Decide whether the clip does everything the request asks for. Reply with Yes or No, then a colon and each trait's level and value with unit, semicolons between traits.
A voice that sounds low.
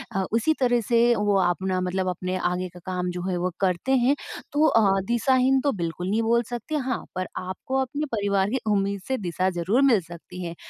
No: high, 200 Hz